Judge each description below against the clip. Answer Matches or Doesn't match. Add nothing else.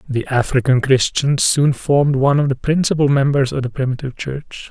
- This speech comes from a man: Matches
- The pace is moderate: Matches